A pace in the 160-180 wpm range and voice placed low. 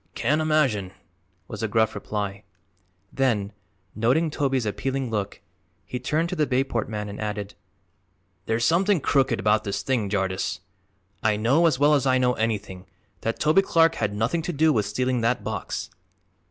Yes: average, 165 wpm; low, 120 Hz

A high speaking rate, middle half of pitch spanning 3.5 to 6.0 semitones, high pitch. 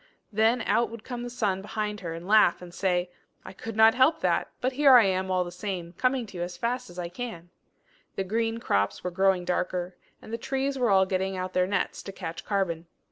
Yes: fast, 230 wpm; average, 4.2 semitones; high, 195 Hz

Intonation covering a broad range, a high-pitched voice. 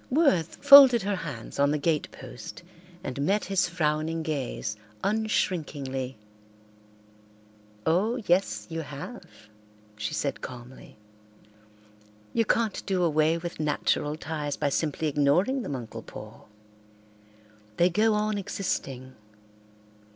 No: wide, 5.8 semitones; medium, 160 Hz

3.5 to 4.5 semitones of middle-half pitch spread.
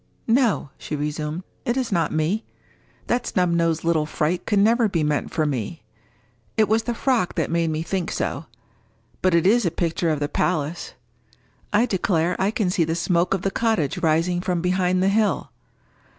Yes: average, 4.1 semitones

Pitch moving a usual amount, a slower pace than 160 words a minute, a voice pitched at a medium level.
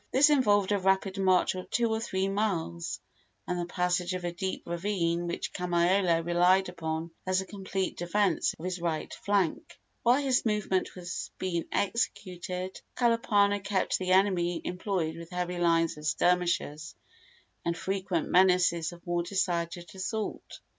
No: narrow, 2.3 semitones; average, 150 wpm; medium, 180 Hz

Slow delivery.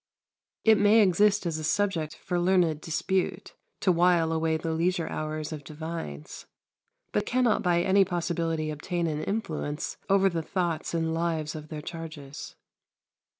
No: average, 150 wpm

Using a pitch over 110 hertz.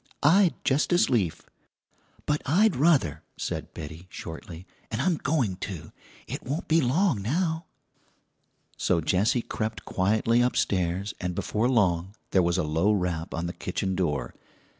No: low, 105 Hz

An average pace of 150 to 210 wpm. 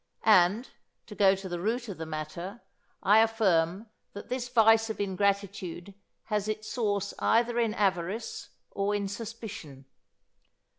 No: average, 140 wpm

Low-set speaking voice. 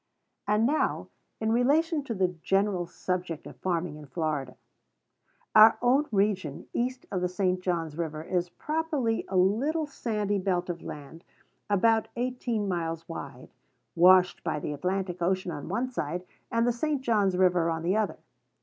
No: high, 190 Hz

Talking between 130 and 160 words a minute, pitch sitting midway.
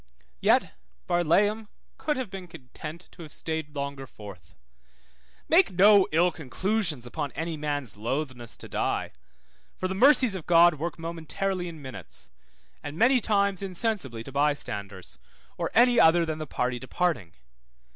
Yes: average, 145 wpm; medium, 165 Hz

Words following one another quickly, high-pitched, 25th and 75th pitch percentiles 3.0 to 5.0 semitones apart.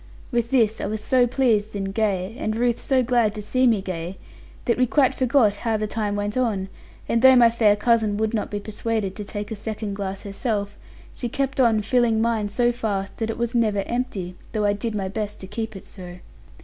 No: fast, 220 wpm; high, 220 Hz; narrow, 2.6 semitones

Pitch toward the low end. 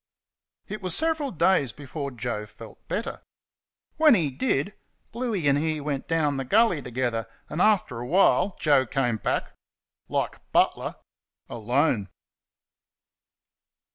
No: medium, 145 Hz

